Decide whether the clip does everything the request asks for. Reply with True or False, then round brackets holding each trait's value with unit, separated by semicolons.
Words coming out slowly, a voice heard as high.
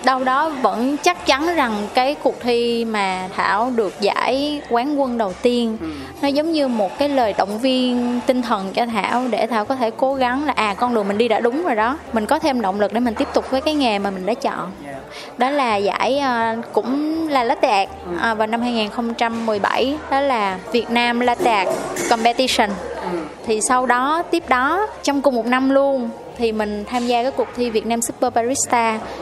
False (205 wpm; 245 Hz)